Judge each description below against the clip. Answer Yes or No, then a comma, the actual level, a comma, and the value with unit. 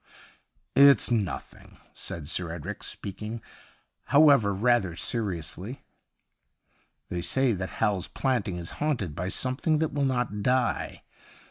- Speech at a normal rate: No, slow, 125 wpm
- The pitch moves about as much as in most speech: No, wide, 6.1 semitones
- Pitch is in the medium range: No, low, 105 Hz